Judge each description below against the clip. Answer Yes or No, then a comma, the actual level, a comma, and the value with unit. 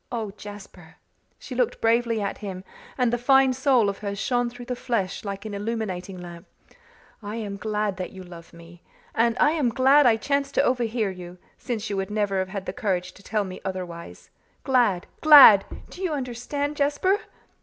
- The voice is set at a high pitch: Yes, high, 215 Hz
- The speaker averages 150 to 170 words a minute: No, average, 185 wpm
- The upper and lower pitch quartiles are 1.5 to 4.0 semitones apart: No, average, 4.5 semitones